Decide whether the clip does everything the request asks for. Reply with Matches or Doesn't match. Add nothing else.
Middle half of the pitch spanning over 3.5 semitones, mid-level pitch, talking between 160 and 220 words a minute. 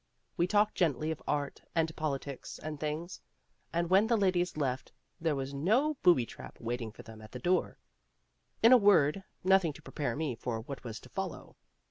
Matches